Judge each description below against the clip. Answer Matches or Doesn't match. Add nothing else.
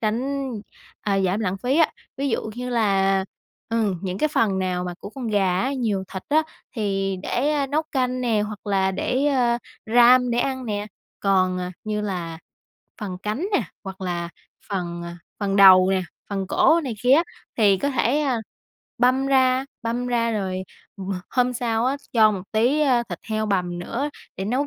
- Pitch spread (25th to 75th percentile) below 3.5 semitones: Doesn't match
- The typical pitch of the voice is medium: Doesn't match